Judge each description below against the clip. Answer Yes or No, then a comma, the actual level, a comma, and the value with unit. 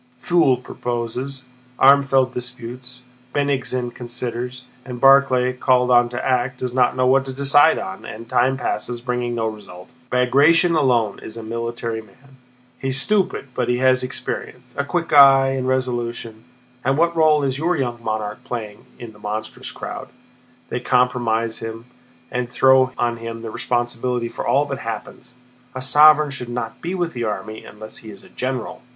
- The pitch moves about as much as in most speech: No, narrow, 2.3 semitones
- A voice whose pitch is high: No, low, 125 Hz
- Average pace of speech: Yes, average, 165 wpm